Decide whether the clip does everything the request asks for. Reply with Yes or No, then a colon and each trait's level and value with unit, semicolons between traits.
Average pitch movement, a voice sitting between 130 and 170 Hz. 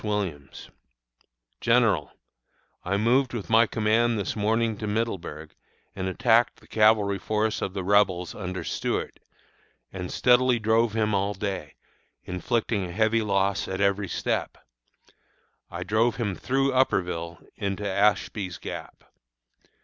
No: average, 3.1 semitones; low, 105 Hz